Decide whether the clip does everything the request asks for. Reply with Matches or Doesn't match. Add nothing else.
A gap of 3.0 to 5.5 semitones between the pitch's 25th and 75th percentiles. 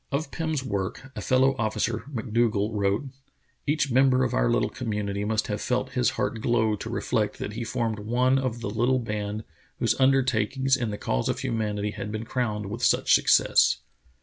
Matches